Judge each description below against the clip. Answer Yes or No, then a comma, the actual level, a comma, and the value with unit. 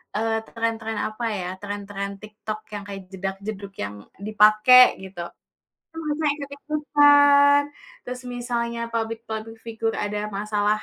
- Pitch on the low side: No, high, 220 Hz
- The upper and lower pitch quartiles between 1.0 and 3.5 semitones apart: Yes, average, 2.8 semitones